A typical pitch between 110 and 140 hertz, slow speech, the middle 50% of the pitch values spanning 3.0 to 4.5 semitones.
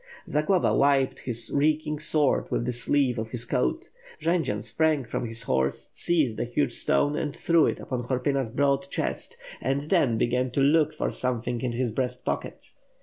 No: low, 135 Hz; average, 175 wpm; average, 3.9 semitones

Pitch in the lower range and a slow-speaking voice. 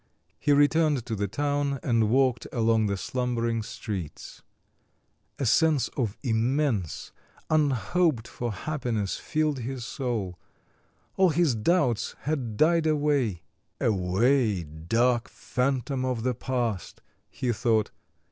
Yes: low, 125 Hz; slow, 115 wpm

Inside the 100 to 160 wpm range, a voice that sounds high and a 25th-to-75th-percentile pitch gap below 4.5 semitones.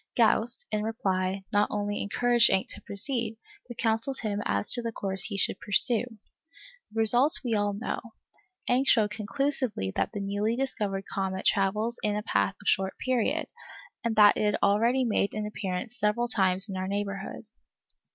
No: average, 170 wpm; high, 210 Hz; average, 2.8 semitones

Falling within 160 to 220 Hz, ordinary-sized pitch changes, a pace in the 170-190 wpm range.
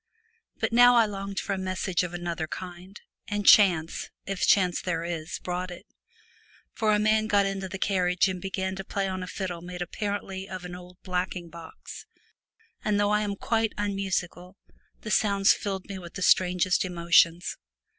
No: high, 190 Hz; narrow, 2.1 semitones; average, 185 wpm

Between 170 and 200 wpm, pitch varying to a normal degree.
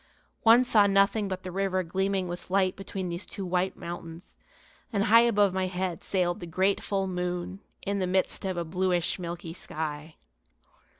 No: average, 175 wpm; narrow, 2.1 semitones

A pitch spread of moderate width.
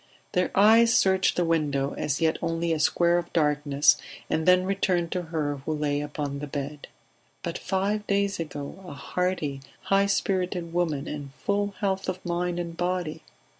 Yes: average, 4.1 semitones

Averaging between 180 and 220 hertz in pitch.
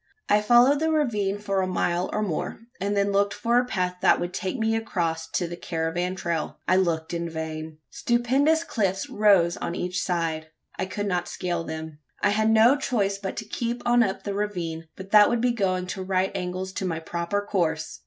Yes: high, 190 Hz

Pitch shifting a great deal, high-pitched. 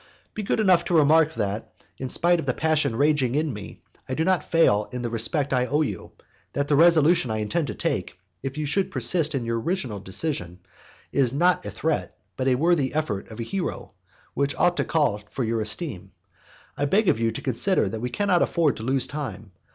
No: wide, 5.9 semitones; medium, 140 Hz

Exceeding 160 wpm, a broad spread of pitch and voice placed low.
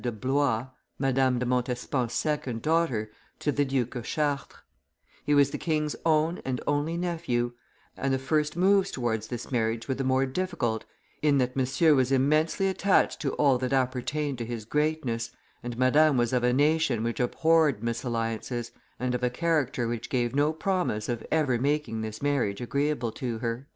No: average, 175 wpm; average, 4.0 semitones; low, 130 Hz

